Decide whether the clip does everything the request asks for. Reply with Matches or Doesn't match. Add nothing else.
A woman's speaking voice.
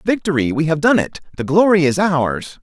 Doesn't match